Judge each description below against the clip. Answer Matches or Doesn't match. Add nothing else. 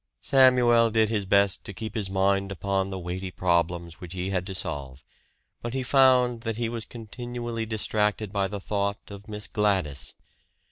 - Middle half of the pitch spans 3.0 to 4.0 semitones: Matches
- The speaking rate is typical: Matches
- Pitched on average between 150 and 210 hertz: Doesn't match